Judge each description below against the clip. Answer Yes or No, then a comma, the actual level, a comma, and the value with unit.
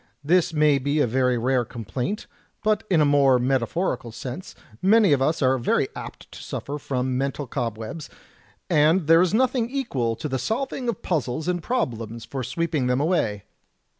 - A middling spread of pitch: No, wide, 5.7 semitones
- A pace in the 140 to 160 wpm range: No, average, 180 wpm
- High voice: No, medium, 140 Hz